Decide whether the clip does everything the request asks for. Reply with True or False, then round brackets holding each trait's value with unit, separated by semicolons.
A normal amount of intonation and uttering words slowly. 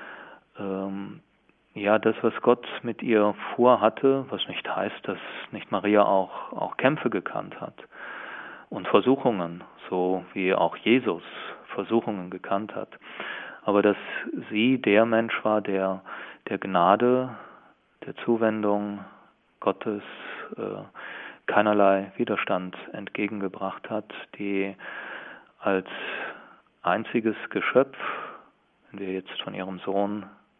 False (2.2 semitones; 105 wpm)